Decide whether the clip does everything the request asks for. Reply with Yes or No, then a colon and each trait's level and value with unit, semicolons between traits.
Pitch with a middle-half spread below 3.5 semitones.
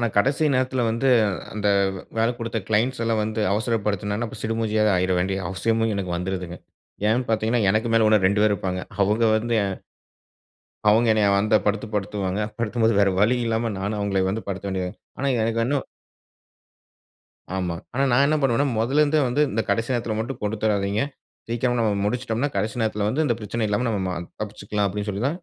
Yes: narrow, 2.5 semitones